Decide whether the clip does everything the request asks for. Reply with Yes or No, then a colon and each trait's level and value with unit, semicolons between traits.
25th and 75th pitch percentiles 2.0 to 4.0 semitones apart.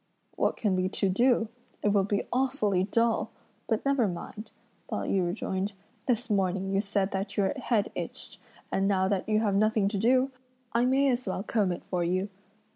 Yes: average, 3.4 semitones